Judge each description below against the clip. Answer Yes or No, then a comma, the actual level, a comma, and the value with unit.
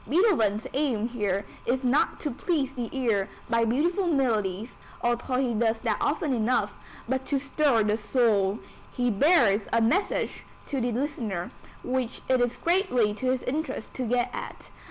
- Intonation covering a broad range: No, average, 3.7 semitones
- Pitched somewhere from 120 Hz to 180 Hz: No, high, 245 Hz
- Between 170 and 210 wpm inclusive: No, average, 160 wpm